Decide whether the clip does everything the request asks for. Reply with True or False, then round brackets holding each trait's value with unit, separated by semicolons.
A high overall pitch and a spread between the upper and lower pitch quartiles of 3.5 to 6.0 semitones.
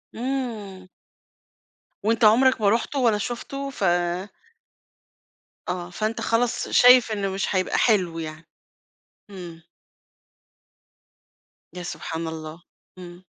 True (200 Hz; 5.1 semitones)